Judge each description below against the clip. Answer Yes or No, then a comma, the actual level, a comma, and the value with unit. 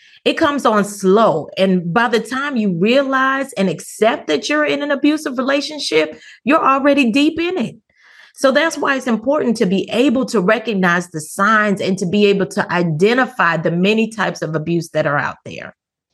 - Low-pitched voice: No, high, 225 Hz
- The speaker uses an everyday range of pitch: No, wide, 6.6 semitones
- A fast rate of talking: No, average, 185 wpm